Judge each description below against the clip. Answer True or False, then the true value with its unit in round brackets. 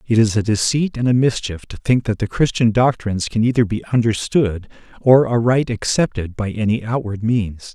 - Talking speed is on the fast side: False (185 wpm)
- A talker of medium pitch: False (115 Hz)